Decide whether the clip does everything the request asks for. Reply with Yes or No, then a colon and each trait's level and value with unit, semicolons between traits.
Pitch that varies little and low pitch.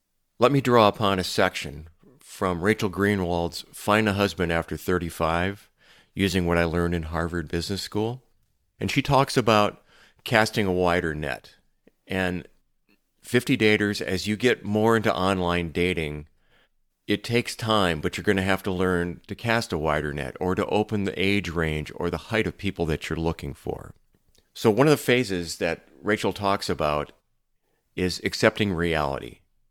No: average, 3.7 semitones; very low, 95 Hz